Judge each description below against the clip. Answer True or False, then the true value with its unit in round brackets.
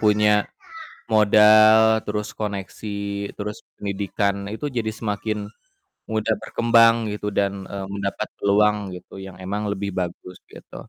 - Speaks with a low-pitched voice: True (105 Hz)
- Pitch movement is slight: True (1.4 semitones)